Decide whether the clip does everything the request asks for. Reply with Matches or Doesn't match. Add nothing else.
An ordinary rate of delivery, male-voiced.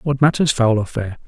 Doesn't match